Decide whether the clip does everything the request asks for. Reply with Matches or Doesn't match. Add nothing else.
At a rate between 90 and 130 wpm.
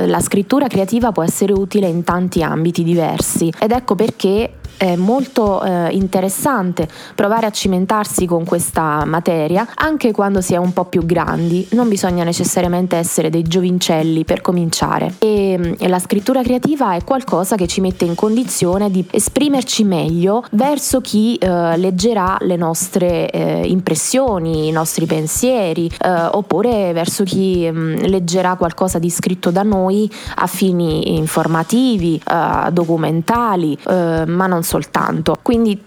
Doesn't match